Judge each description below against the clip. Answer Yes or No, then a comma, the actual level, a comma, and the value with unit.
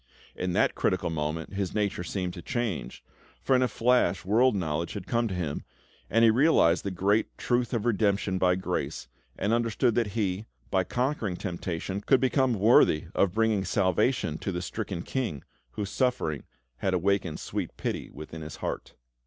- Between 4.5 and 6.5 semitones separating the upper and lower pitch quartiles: Yes, average, 4.8 semitones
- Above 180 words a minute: No, average, 170 wpm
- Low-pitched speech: Yes, low, 100 Hz